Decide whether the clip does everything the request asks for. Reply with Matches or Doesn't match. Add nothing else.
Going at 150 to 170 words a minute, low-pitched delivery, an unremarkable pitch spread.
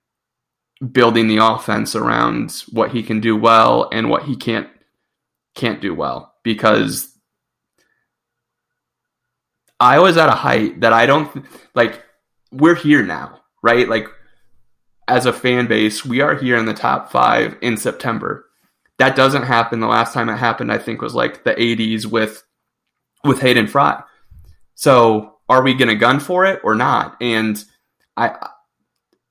Matches